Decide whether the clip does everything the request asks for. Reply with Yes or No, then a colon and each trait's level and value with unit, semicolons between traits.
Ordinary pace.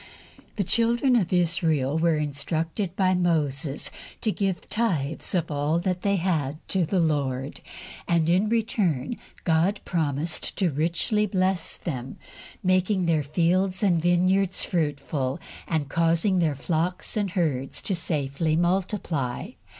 No: slow, 125 wpm